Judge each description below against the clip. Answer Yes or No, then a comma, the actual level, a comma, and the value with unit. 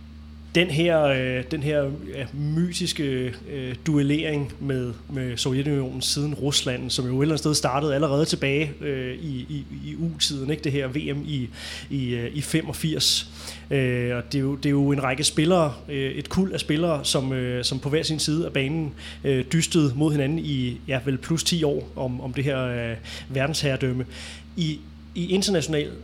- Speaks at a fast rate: No, average, 185 wpm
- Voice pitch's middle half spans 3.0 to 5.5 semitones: Yes, average, 3.3 semitones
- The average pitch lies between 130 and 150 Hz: Yes, medium, 140 Hz